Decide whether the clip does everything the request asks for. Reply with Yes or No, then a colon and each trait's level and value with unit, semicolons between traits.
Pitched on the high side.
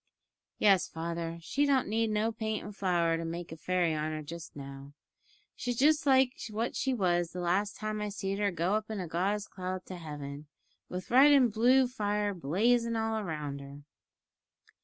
Yes: high, 195 Hz